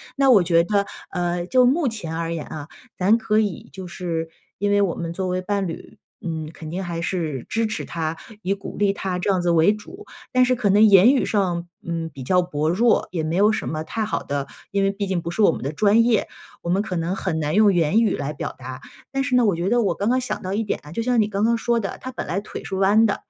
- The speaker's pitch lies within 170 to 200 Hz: Yes, high, 190 Hz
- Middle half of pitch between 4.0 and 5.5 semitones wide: Yes, average, 4.3 semitones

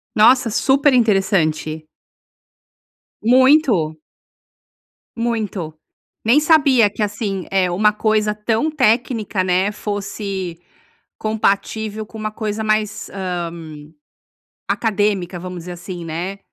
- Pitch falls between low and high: No, high, 210 Hz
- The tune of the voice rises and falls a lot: No, average, 3.4 semitones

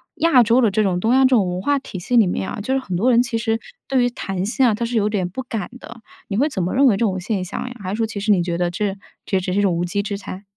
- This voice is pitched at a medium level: No, high, 210 Hz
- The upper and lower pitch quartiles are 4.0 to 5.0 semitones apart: Yes, average, 4.4 semitones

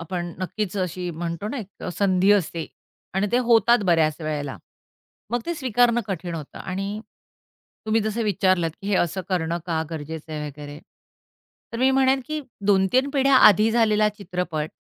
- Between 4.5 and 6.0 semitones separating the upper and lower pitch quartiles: Yes, average, 5.0 semitones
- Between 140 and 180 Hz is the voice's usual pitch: No, high, 190 Hz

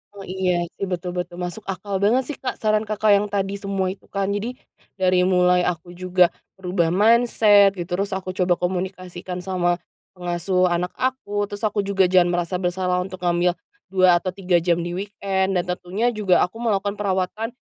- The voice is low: No, medium, 185 Hz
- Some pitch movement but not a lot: No, narrow, 2.1 semitones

